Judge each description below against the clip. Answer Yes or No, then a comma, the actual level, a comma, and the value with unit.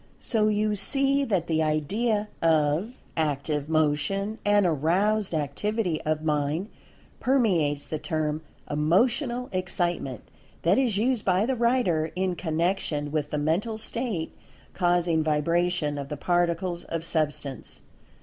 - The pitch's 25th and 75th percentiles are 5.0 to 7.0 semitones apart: Yes, wide, 5.4 semitones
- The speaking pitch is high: No, medium, 175 Hz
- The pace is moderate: No, slow, 125 wpm